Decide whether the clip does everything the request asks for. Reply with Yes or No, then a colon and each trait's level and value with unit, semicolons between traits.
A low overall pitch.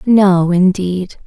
No: high, 190 Hz